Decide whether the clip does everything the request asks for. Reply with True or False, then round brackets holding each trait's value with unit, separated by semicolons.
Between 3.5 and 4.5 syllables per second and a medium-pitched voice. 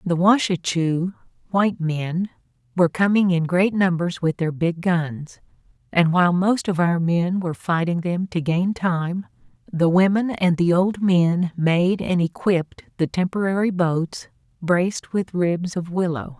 True (4.3 syllables/s; 175 Hz)